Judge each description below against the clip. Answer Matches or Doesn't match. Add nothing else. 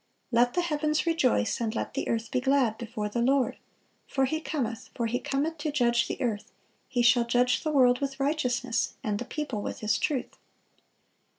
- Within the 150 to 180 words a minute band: Doesn't match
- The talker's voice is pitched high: Matches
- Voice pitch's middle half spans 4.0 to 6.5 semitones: Doesn't match